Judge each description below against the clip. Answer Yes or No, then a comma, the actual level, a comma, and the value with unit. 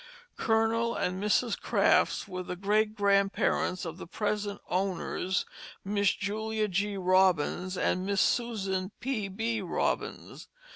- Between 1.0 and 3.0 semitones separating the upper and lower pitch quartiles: Yes, narrow, 2.6 semitones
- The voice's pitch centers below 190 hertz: No, high, 200 Hz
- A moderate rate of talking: No, slow, 125 wpm